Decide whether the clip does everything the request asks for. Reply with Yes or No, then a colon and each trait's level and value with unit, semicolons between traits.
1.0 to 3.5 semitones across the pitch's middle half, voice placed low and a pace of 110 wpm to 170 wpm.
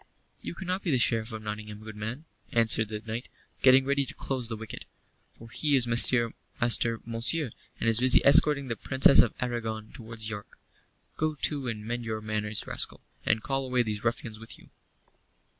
No: average, 3.1 semitones; low, 115 Hz; average, 180 wpm